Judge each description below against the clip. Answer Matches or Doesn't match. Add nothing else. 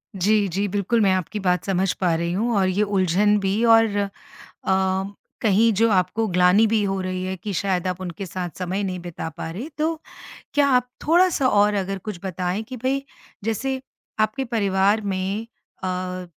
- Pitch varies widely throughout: Doesn't match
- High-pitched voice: Matches